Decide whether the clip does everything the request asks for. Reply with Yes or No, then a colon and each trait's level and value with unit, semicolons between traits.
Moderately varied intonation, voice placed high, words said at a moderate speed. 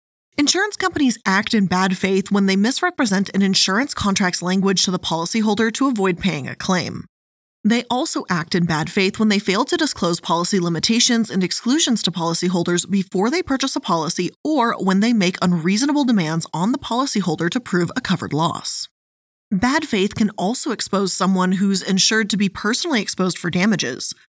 Yes: average, 4.5 semitones; high, 195 Hz; average, 175 wpm